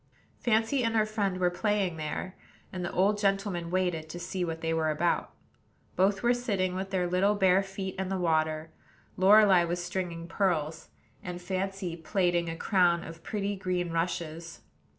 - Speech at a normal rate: Yes, average, 170 wpm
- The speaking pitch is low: No, medium, 185 Hz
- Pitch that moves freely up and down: No, narrow, 2.5 semitones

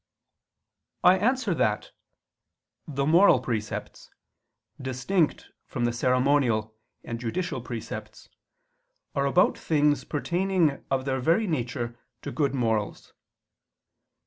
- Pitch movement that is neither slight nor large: No, wide, 5.8 semitones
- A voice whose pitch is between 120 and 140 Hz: Yes, low, 135 Hz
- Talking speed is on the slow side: Yes, slow, 100 wpm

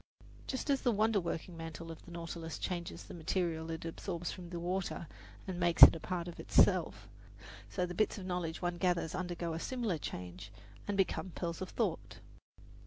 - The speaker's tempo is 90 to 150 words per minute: No, average, 185 wpm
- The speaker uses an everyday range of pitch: No, narrow, 1.9 semitones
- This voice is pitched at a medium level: Yes, medium, 175 Hz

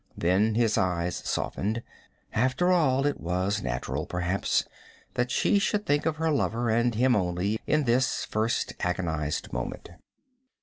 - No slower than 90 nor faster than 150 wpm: Yes, average, 145 wpm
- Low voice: Yes, low, 110 Hz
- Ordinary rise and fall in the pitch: No, wide, 6.6 semitones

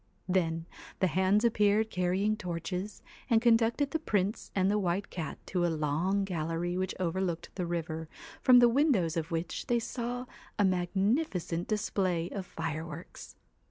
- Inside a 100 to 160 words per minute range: Yes, average, 150 wpm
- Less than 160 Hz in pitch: No, medium, 185 Hz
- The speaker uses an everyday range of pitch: Yes, average, 4.0 semitones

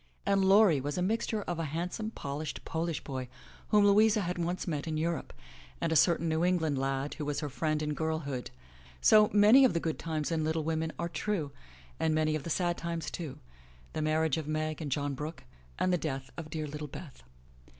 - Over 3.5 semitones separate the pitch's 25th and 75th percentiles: No, average, 2.8 semitones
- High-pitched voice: No, medium, 160 Hz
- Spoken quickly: Yes, fast, 210 wpm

